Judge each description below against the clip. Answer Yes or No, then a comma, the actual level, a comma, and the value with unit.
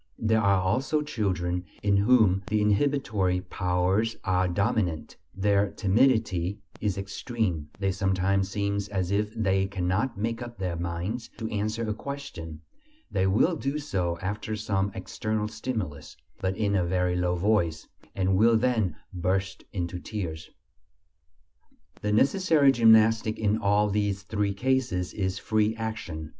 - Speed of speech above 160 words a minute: No, average, 140 wpm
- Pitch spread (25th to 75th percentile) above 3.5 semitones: No, average, 3.2 semitones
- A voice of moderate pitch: No, low, 100 Hz